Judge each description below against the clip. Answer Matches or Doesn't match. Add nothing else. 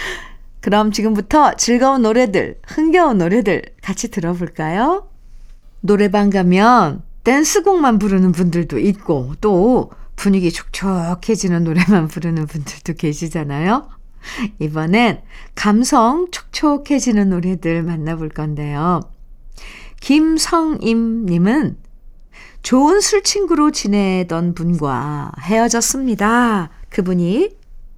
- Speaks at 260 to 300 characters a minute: Doesn't match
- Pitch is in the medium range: Doesn't match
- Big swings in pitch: Matches